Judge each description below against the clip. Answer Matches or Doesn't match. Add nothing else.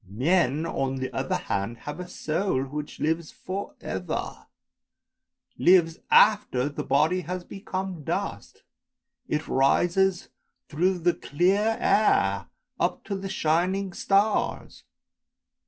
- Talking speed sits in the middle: Doesn't match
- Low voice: Doesn't match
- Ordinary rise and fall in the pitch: Matches